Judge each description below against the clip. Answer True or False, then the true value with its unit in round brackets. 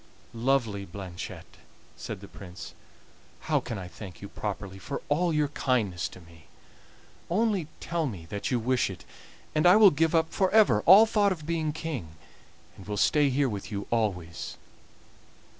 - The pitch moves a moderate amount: False (8.7 semitones)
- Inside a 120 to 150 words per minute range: False (165 wpm)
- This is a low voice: True (125 Hz)